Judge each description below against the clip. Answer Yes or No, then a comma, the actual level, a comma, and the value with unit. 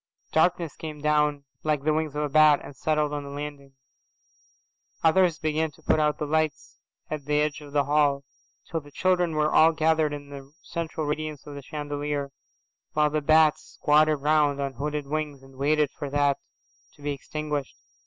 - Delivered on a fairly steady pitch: Yes, narrow, 1.3 semitones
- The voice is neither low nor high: Yes, medium, 150 Hz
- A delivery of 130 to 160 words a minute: No, average, 185 wpm